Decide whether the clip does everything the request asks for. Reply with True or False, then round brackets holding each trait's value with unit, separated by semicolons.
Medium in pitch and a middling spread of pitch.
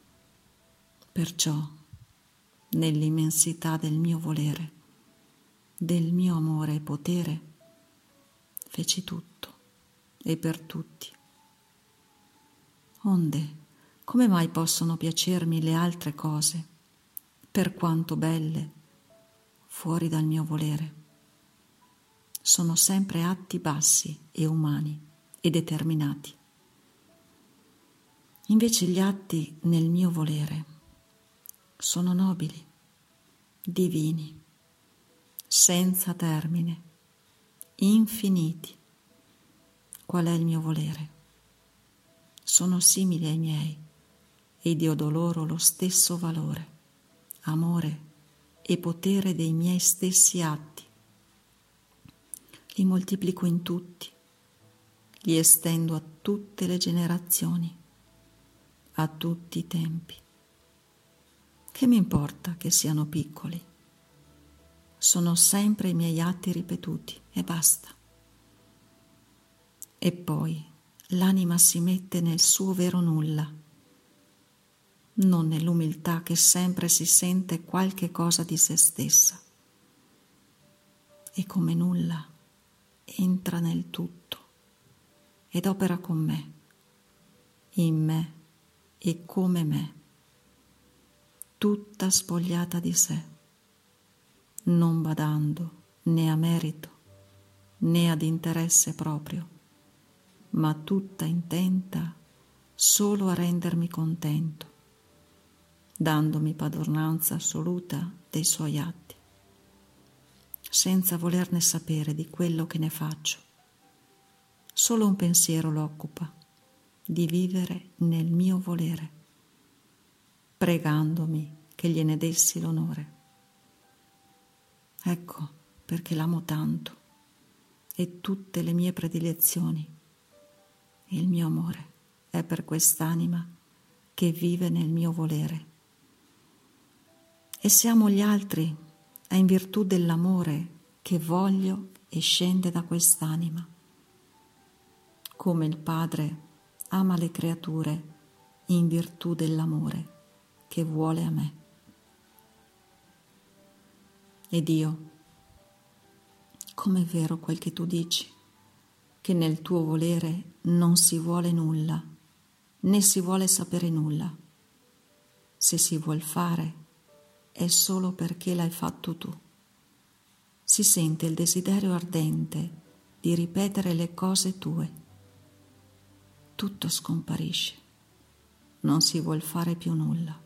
False (165 Hz; 2.1 semitones)